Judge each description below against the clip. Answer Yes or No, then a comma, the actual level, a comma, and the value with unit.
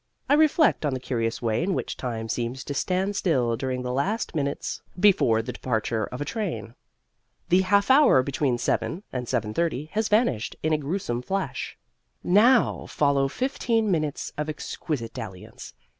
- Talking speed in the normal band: Yes, average, 160 wpm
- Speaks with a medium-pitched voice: Yes, medium, 145 Hz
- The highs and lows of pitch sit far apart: Yes, wide, 7.9 semitones